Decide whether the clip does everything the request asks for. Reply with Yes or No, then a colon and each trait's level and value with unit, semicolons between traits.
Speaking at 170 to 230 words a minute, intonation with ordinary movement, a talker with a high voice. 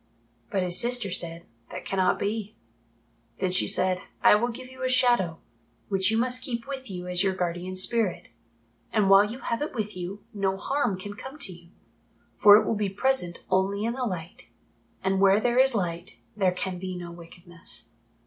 Yes: average, 190 wpm; average, 4.4 semitones; high, 195 Hz